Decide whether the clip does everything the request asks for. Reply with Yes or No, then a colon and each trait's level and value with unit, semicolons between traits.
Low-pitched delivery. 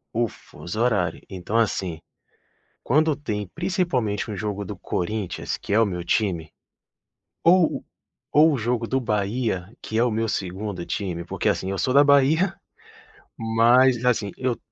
Yes: low, 110 Hz